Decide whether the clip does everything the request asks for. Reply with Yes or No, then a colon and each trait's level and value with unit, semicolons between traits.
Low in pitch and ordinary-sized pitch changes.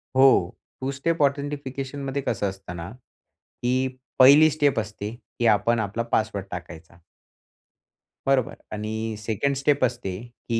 Yes: low, 120 Hz; average, 4.7 semitones